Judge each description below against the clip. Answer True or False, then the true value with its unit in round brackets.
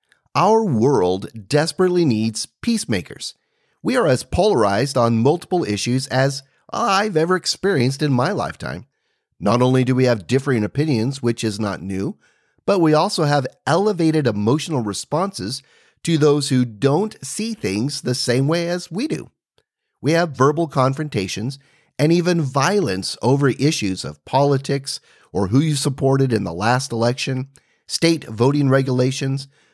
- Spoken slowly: False (145 wpm)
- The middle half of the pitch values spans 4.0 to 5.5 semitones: True (4.8 semitones)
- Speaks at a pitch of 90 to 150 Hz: True (135 Hz)